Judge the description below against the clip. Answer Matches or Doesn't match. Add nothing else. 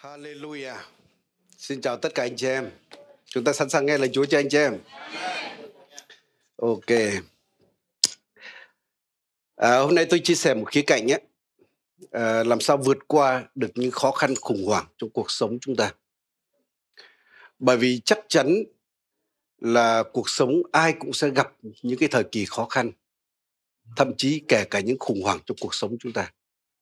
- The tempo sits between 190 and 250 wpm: Doesn't match